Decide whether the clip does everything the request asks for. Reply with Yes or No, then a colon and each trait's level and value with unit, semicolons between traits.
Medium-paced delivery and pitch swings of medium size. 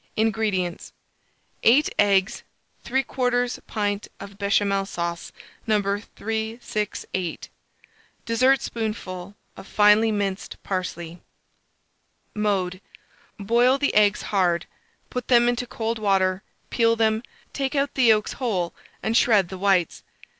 No: slow, 105 wpm; average, 3.0 semitones